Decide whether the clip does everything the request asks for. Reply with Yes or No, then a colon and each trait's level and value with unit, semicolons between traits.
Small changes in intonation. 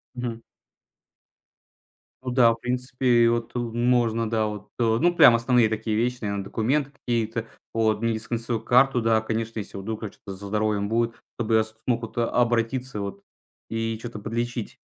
Yes: narrow, 1.6 semitones